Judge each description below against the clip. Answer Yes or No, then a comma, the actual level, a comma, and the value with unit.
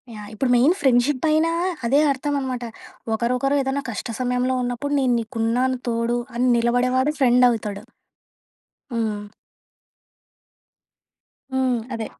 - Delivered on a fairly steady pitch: Yes, narrow, 2.2 semitones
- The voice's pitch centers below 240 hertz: No, very high, 250 Hz